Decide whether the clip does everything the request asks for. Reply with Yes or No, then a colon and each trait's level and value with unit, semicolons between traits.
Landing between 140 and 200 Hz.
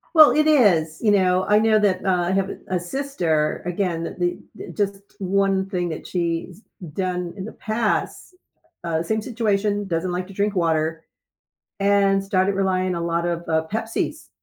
Yes: high, 190 Hz